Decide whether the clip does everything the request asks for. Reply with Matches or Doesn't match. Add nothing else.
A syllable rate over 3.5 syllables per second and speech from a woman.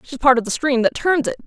Matches